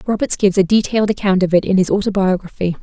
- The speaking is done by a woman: Yes, female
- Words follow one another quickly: Yes, fast, 210 wpm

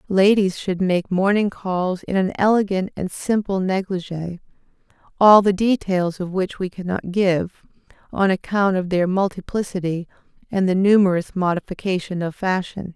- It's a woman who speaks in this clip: Yes, female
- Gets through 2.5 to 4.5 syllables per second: No, 4.7 syllables/s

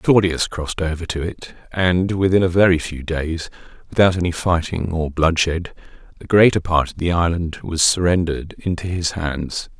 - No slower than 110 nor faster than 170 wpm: Yes, average, 165 wpm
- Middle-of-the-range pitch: No, very low, 85 Hz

